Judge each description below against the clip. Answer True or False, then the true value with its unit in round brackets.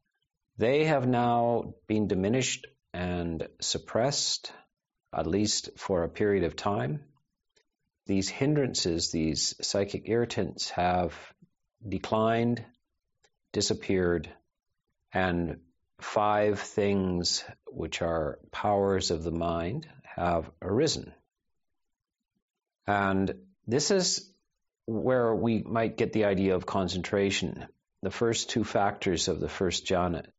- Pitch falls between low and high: False (100 Hz)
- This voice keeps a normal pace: False (105 wpm)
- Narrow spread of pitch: False (4.7 semitones)